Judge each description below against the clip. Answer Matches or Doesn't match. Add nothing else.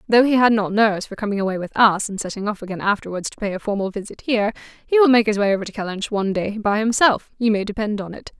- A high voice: Matches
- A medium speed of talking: Doesn't match